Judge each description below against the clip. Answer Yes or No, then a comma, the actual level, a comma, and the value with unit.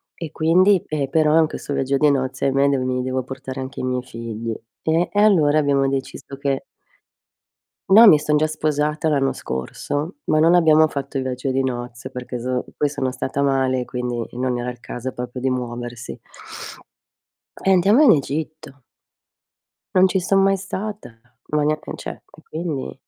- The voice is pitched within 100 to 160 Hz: Yes, medium, 140 Hz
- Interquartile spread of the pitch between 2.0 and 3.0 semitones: No, average, 3.5 semitones